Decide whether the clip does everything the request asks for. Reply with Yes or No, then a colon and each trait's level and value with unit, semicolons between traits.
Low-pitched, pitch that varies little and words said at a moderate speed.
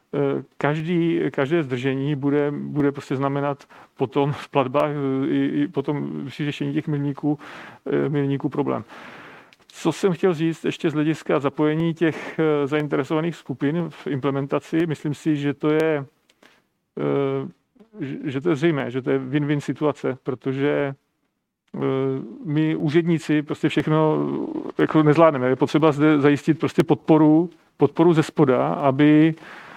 No: medium, 150 Hz; narrow, 2.0 semitones; average, 125 wpm